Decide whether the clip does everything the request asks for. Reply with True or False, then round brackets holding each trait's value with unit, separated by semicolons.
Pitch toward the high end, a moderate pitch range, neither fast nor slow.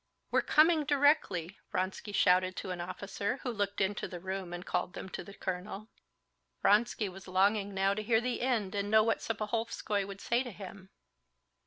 True (200 Hz; 3.0 semitones; 185 wpm)